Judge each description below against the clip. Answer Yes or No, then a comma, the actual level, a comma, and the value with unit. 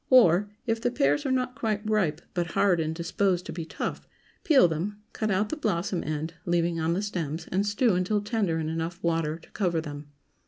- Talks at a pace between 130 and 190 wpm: No, fast, 205 wpm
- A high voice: No, medium, 180 Hz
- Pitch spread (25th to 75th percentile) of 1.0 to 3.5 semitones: No, average, 4.4 semitones